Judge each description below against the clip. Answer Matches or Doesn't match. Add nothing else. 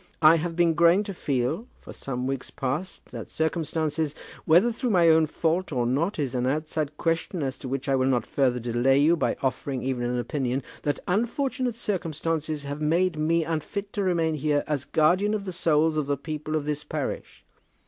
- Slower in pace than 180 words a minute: Doesn't match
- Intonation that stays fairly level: Doesn't match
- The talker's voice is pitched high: Doesn't match